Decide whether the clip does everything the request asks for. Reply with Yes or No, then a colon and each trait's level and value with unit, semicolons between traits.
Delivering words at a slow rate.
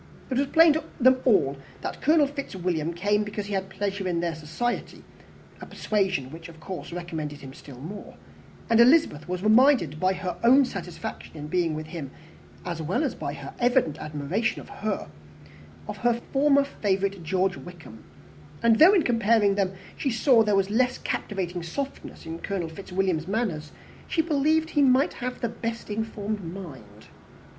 No: average, 165 wpm